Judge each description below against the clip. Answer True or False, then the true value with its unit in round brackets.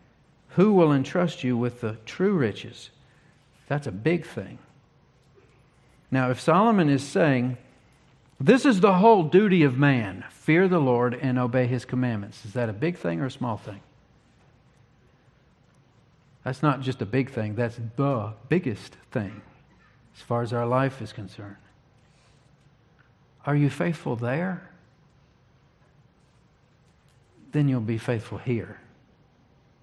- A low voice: True (130 Hz)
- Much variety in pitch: False (3.7 semitones)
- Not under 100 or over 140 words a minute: True (135 wpm)